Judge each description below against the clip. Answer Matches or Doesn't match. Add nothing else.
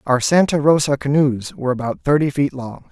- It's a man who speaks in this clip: Matches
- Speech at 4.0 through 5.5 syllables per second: Matches